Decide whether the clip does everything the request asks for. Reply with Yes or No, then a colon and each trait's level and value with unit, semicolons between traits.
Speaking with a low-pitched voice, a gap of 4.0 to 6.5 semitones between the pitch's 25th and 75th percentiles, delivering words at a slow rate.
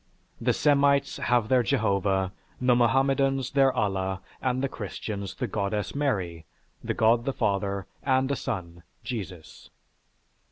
Yes: low, 115 Hz; wide, 5.4 semitones; slow, 130 wpm